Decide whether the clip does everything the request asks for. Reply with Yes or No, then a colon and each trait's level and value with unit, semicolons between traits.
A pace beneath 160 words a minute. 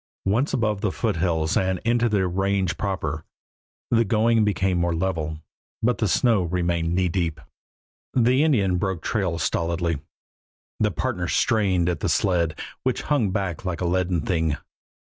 Yes: average, 150 wpm